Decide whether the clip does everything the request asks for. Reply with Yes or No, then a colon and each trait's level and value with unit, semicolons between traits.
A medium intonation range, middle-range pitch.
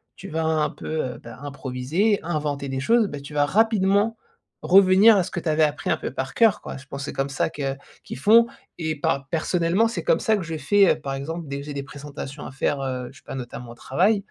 No: wide, 5.7 semitones; medium, 155 Hz